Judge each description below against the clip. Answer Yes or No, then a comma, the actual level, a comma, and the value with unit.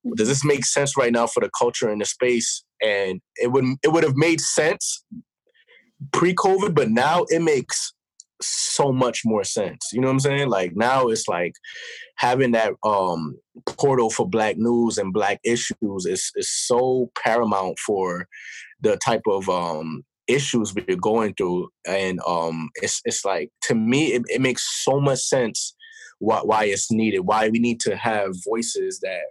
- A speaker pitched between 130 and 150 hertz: Yes, low, 135 Hz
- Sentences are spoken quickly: No, average, 175 wpm